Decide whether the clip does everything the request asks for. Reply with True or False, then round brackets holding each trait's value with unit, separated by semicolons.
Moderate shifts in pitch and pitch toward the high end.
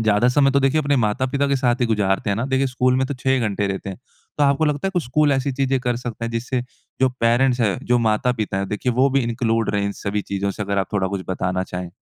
False (4.5 semitones; 120 Hz)